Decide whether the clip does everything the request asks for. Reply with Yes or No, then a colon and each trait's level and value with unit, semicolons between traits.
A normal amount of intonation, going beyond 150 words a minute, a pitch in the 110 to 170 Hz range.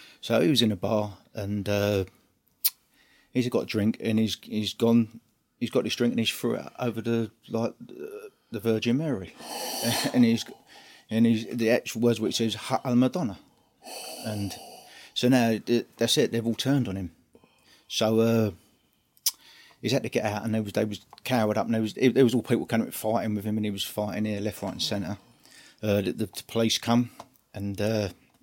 No: narrow, 1.9 semitones; average, 200 wpm; low, 115 Hz